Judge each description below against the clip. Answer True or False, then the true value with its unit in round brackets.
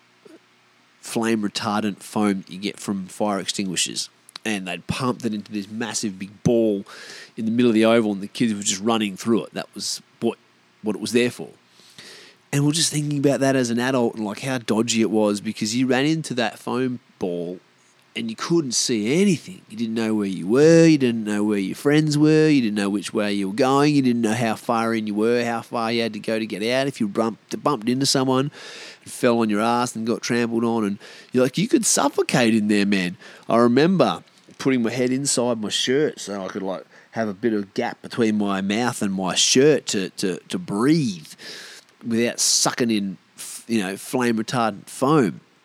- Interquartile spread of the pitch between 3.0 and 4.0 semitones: True (3.4 semitones)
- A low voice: True (115 Hz)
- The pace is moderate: False (215 wpm)